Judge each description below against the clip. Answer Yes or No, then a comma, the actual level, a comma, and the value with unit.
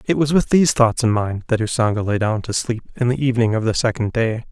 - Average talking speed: No, fast, 265 wpm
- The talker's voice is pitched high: No, low, 120 Hz